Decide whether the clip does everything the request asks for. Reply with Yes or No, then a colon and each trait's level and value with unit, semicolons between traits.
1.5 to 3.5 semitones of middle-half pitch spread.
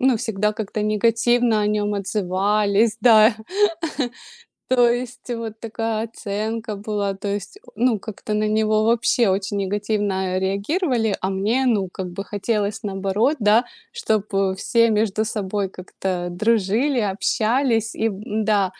Yes: narrow, 2.4 semitones